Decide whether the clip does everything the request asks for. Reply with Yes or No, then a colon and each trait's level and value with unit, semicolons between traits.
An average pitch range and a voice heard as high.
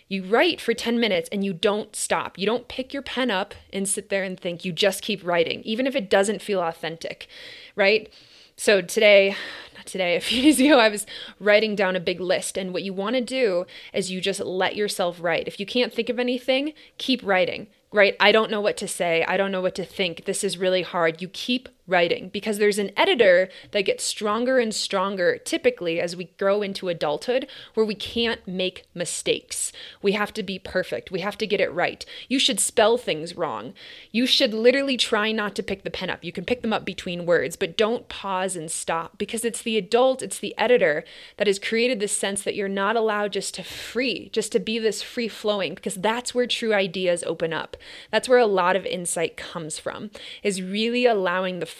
Yes: average, 4.2 semitones; high, 210 Hz